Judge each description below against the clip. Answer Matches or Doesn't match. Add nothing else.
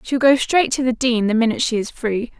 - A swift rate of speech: Matches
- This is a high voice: Matches